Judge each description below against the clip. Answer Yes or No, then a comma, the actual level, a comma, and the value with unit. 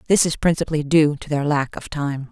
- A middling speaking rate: No, fast, 235 wpm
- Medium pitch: Yes, medium, 150 Hz